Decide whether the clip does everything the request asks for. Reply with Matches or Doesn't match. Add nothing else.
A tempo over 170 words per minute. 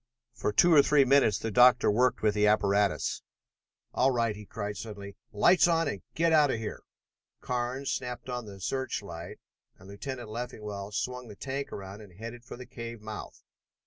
Matches